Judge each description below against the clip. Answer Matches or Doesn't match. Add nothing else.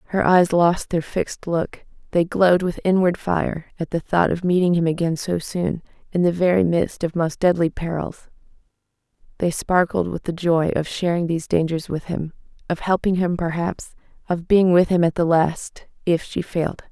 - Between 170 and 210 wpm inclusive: Matches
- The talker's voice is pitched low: Doesn't match